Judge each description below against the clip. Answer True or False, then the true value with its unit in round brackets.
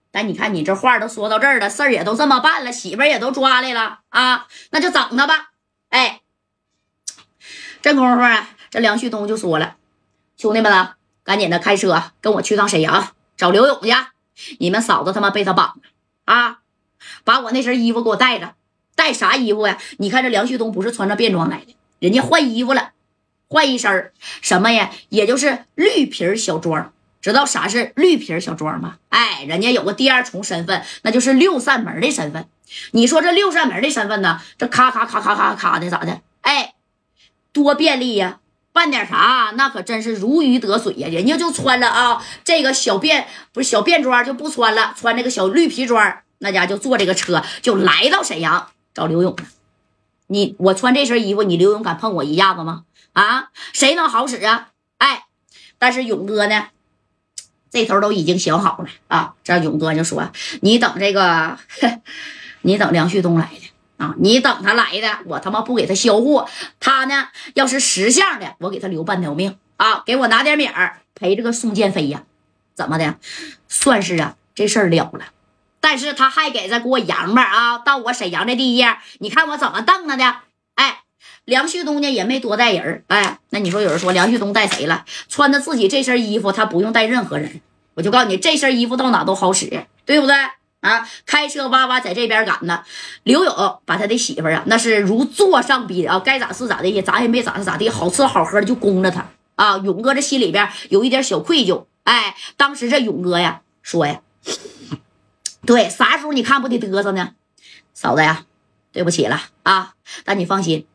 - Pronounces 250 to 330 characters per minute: True (280 characters per minute)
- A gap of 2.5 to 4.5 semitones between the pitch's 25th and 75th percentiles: False (5.4 semitones)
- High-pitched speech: True (230 Hz)